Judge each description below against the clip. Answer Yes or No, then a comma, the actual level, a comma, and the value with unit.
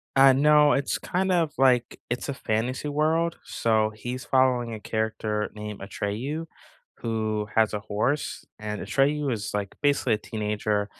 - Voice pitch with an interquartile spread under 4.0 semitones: No, average, 4.9 semitones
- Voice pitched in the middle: No, low, 120 Hz